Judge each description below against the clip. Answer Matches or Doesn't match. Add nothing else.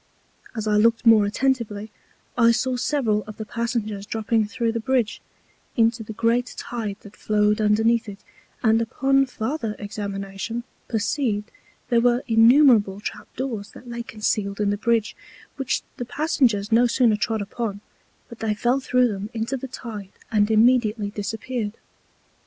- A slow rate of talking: Doesn't match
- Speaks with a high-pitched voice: Matches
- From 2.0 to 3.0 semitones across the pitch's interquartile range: Matches